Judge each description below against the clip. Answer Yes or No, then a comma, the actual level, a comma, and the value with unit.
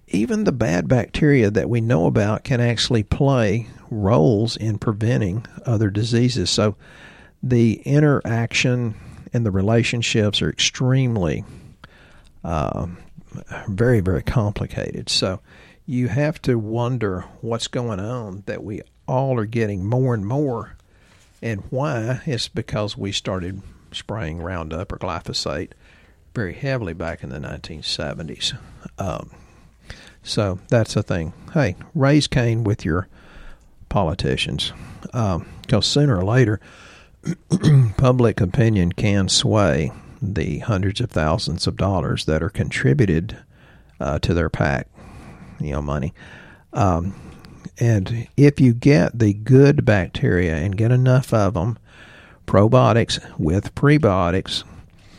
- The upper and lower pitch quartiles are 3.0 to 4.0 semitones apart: No, average, 4.6 semitones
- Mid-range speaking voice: No, low, 115 Hz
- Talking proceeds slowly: Yes, slow, 120 wpm